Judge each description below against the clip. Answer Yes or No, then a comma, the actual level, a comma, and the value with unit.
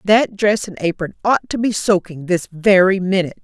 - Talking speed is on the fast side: No, average, 190 wpm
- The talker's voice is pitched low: No, high, 190 Hz